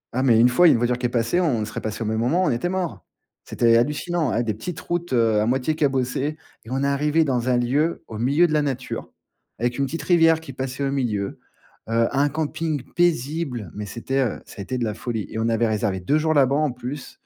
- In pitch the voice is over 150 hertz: No, low, 130 Hz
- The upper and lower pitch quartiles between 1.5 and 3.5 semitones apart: No, average, 4.8 semitones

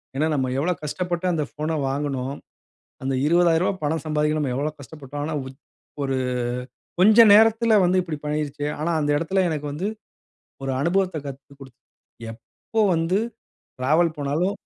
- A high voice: No, medium, 155 Hz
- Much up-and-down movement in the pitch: No, average, 3.8 semitones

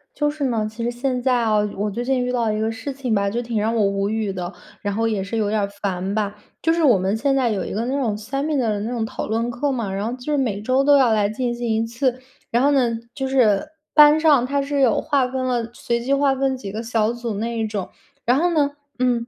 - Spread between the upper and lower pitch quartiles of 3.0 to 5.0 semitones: Yes, average, 3.7 semitones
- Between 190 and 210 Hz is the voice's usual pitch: No, high, 235 Hz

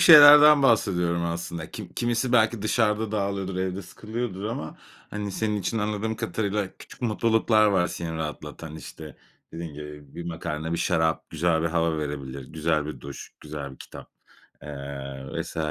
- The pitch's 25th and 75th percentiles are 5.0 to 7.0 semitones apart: Yes, wide, 5.5 semitones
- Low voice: Yes, very low, 90 Hz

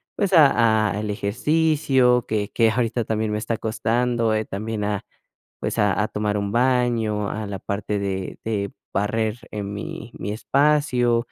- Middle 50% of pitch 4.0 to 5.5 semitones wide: No, average, 2.8 semitones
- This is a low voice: Yes, low, 110 Hz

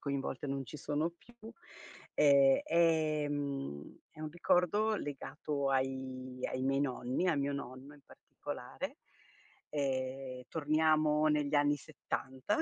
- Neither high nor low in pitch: Yes, medium, 145 Hz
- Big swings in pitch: No, narrow, 2.4 semitones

